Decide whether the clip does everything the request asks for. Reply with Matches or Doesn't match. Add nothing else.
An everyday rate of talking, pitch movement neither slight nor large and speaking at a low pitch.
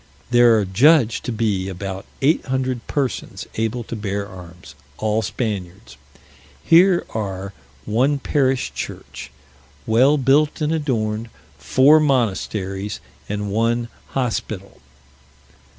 Doesn't match